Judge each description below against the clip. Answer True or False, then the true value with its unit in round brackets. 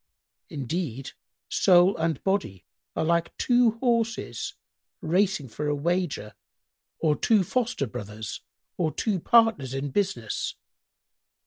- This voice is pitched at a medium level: True (170 Hz)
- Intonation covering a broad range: True (7.0 semitones)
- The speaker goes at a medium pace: False (110 wpm)